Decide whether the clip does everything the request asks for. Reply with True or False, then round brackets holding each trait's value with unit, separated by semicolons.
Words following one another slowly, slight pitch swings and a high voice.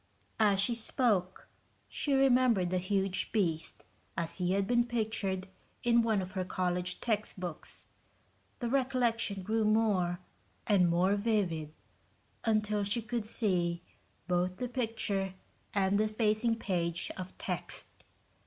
False (125 wpm; 3.7 semitones; 205 Hz)